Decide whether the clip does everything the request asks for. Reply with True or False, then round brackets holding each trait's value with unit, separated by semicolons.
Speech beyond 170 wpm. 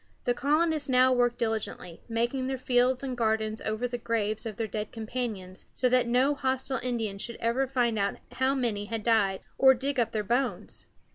True (190 wpm)